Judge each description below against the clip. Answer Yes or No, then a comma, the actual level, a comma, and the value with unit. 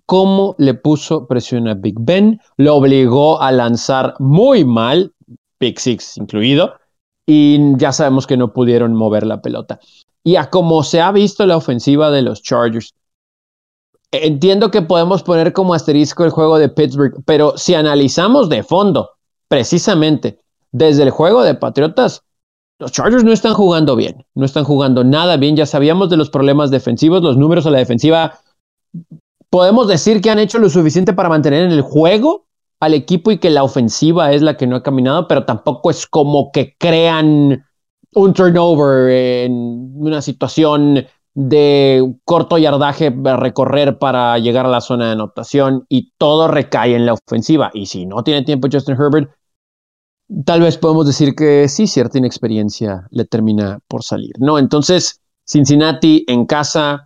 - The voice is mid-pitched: Yes, medium, 145 Hz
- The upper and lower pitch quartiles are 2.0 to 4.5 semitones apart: Yes, average, 4.2 semitones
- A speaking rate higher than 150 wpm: Yes, average, 165 wpm